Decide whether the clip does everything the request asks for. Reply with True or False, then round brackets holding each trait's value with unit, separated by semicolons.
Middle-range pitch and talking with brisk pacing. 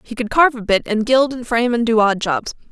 False (235 Hz; 285 wpm)